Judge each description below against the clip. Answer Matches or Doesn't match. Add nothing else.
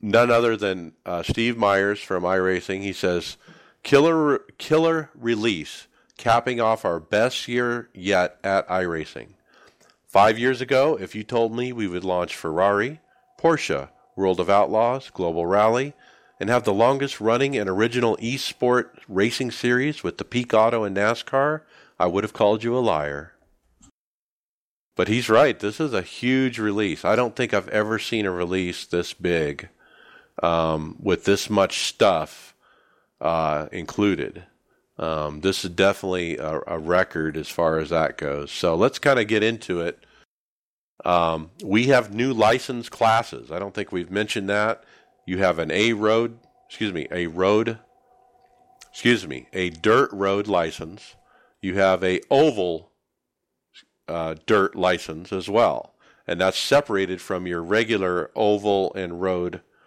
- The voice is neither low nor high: Doesn't match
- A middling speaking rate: Matches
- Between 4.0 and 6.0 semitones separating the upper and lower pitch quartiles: Matches